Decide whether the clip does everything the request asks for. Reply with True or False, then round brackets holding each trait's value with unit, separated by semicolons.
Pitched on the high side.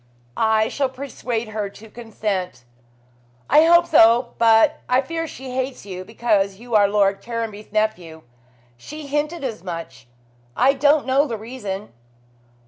True (230 Hz)